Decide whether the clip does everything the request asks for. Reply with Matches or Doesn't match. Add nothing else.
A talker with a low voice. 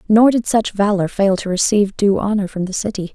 Doesn't match